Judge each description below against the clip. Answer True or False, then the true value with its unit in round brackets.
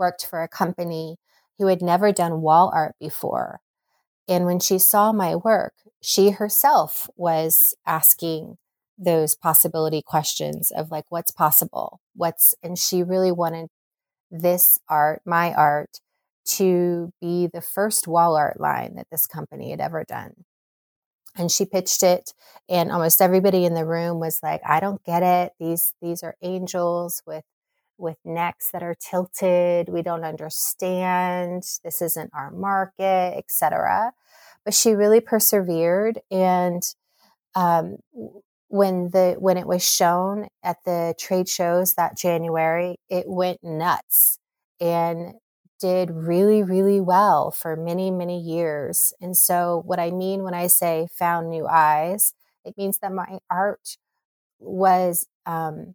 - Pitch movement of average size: False (2.1 semitones)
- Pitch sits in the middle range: True (175 Hz)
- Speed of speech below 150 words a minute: True (140 wpm)